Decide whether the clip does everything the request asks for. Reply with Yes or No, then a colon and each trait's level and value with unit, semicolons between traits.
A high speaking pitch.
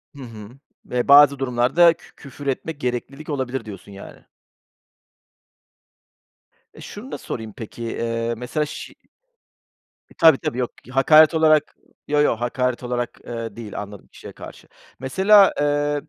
No: low, 130 Hz